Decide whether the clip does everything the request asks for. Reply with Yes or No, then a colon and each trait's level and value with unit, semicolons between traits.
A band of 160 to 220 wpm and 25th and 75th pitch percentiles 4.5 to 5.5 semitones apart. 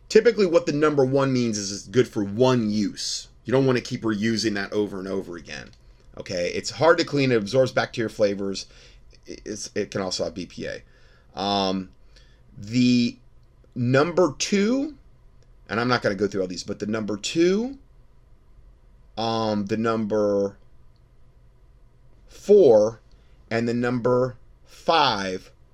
No: average, 145 wpm; average, 4.8 semitones